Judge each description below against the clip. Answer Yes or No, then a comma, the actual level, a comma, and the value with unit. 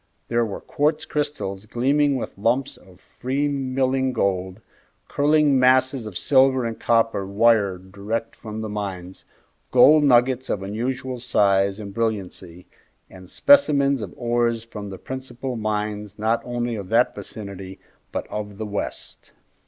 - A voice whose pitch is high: No, low, 115 Hz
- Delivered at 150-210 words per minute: No, average, 140 wpm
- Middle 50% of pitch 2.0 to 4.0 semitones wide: No, average, 4.6 semitones